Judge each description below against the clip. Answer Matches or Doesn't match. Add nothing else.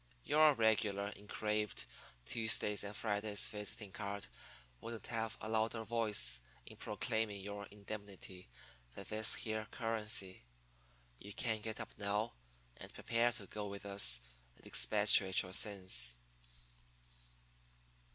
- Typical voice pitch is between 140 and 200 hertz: Doesn't match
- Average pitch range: Doesn't match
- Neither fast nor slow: Doesn't match